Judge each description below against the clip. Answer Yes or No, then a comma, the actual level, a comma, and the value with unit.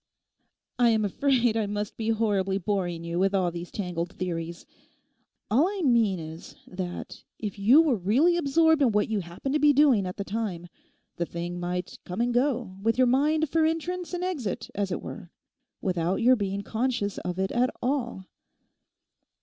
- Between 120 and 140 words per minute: No, average, 180 wpm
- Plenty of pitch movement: Yes, wide, 6.2 semitones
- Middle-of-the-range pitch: No, high, 210 Hz